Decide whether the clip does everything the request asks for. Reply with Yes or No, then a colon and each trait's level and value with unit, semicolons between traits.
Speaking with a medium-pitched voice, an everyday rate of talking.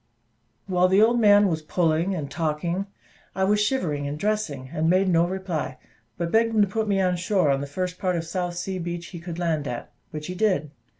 No: medium, 180 Hz; fast, 220 wpm